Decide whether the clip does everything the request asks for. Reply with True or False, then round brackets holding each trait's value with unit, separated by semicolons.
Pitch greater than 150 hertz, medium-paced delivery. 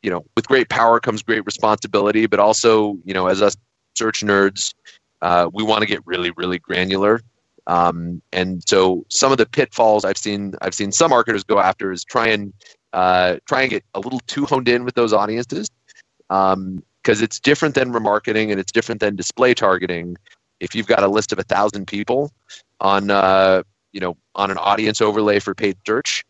False (100 Hz; 190 wpm)